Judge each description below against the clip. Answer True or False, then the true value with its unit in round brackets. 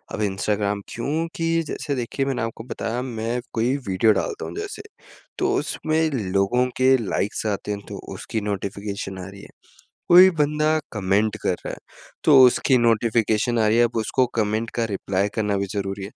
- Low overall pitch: True (115 Hz)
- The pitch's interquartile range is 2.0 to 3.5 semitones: False (4.0 semitones)